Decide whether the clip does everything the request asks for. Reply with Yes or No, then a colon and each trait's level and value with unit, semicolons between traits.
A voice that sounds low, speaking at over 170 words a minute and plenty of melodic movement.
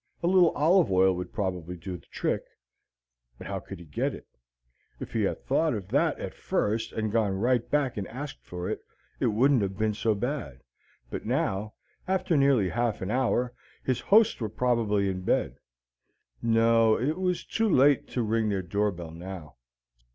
Yes: low, 110 Hz; average, 180 wpm; wide, 5.9 semitones